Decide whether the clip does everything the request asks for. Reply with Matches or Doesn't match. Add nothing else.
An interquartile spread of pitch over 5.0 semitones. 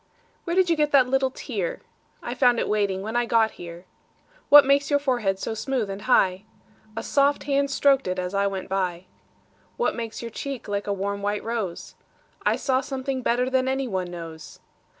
Matches